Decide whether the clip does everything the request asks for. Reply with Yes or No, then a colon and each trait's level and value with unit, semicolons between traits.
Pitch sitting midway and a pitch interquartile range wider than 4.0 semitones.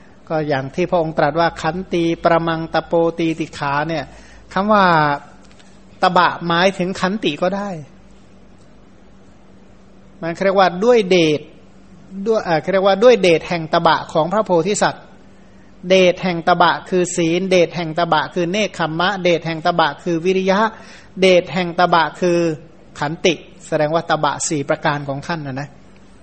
No: medium, 170 Hz; narrow, 2.6 semitones